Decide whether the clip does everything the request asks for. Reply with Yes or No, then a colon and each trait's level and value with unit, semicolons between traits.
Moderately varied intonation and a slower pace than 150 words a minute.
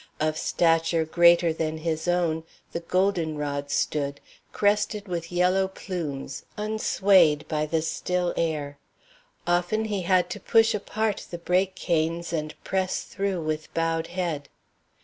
Yes: average, 3.0 semitones; slow, 135 wpm